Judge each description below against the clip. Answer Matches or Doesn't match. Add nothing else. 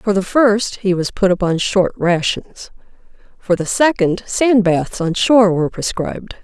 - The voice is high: Matches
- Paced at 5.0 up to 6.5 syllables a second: Doesn't match